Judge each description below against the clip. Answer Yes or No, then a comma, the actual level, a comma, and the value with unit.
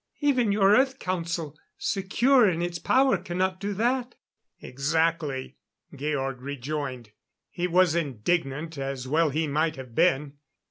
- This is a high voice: No, medium, 165 Hz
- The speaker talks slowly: Yes, slow, 130 wpm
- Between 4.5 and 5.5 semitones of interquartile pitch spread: Yes, average, 5.2 semitones